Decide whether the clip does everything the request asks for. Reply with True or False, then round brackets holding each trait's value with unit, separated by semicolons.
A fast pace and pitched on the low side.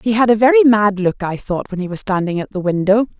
False (280 wpm; 210 Hz)